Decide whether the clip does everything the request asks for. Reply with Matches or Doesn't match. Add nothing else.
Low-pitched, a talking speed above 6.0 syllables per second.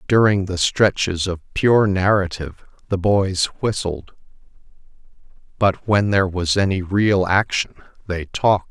Doesn't match